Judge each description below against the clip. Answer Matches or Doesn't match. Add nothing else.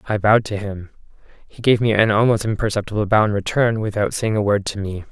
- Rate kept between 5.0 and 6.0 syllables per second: Doesn't match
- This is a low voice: Matches